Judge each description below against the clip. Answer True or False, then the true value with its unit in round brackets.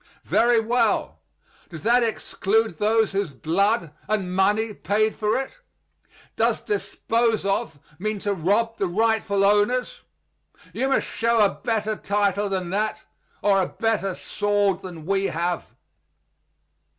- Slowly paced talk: True (130 wpm)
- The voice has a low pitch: False (205 Hz)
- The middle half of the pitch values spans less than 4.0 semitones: True (2.5 semitones)